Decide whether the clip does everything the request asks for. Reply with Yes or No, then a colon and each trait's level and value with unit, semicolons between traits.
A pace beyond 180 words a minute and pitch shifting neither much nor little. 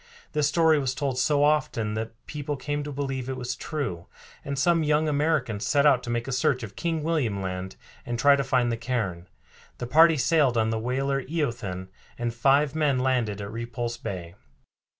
Yes: average, 190 wpm; average, 4.1 semitones